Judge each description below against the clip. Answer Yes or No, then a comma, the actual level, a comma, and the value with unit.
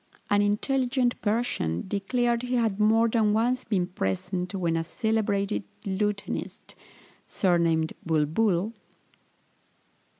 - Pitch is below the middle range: No, high, 205 Hz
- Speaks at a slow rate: Yes, slow, 105 wpm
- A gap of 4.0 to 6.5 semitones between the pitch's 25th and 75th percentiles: Yes, average, 4.5 semitones